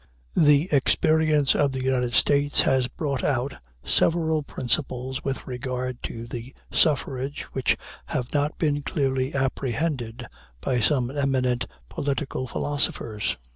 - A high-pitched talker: No, low, 135 Hz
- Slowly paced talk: Yes, slow, 120 wpm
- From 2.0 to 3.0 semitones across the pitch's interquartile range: Yes, narrow, 2.4 semitones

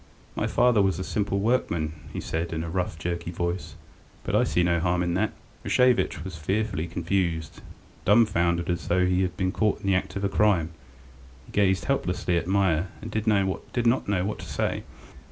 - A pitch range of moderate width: Yes, average, 3.0 semitones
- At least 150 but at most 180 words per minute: No, average, 190 wpm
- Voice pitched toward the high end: No, very low, 95 Hz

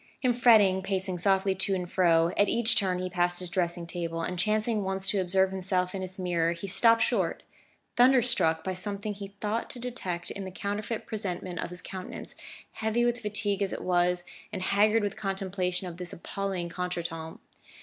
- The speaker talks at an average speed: Yes, average, 190 wpm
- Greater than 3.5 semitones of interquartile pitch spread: No, narrow, 2.5 semitones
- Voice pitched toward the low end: No, high, 190 Hz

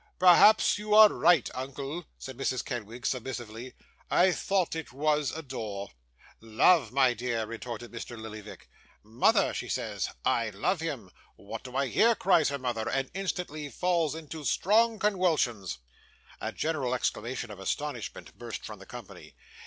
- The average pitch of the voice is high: No, low, 135 Hz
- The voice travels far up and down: Yes, wide, 6.0 semitones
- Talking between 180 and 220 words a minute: No, average, 145 wpm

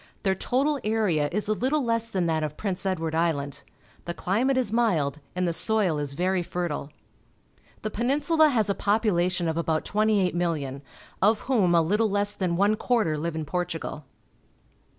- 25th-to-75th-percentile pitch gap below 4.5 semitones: No, average, 5.0 semitones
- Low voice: No, medium, 185 Hz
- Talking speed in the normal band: Yes, average, 170 wpm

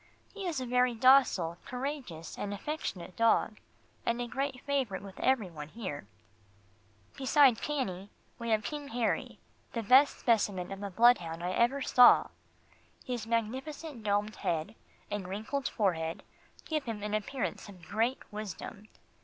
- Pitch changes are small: No, average, 4.9 semitones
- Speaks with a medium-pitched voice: No, high, 225 Hz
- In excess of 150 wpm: No, average, 145 wpm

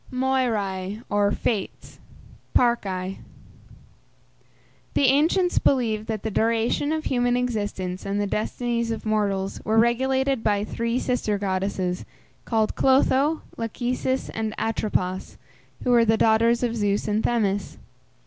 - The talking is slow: Yes, slow, 120 wpm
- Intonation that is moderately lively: Yes, average, 3.3 semitones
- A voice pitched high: Yes, high, 225 Hz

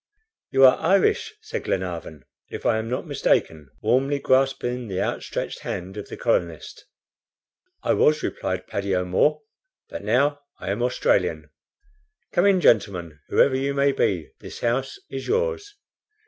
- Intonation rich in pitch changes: Yes, wide, 7.1 semitones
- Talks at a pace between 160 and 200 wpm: No, average, 145 wpm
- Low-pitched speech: Yes, low, 125 Hz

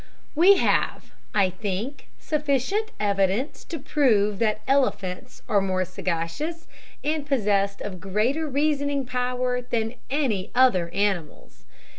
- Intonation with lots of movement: Yes, wide, 6.4 semitones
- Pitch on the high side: Yes, high, 235 Hz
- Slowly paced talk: Yes, slow, 115 wpm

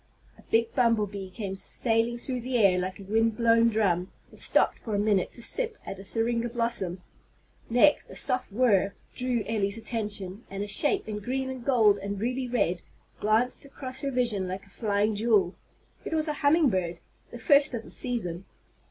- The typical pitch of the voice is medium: No, high, 225 Hz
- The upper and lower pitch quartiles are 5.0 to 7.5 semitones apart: No, average, 3.8 semitones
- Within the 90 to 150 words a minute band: No, average, 190 wpm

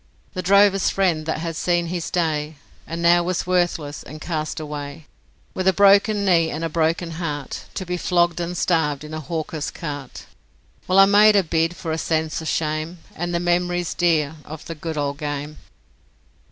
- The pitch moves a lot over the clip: No, narrow, 2.4 semitones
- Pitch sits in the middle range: Yes, medium, 165 Hz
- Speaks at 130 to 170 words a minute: No, average, 185 wpm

